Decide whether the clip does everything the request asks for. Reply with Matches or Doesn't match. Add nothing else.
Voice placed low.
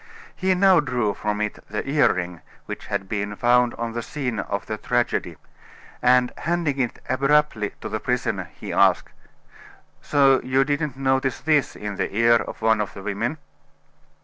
Matches